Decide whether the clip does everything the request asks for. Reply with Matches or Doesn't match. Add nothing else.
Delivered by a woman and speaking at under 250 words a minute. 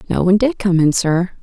Doesn't match